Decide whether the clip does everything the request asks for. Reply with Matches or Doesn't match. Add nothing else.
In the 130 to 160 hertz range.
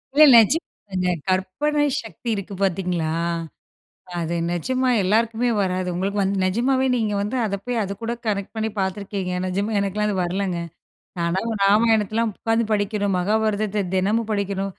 Doesn't match